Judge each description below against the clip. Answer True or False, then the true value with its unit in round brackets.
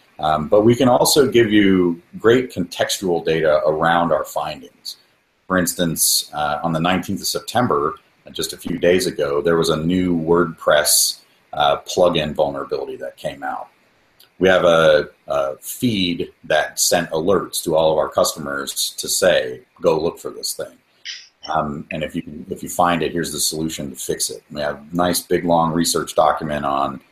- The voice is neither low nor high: False (85 Hz)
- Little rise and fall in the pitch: False (3.2 semitones)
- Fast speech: False (175 wpm)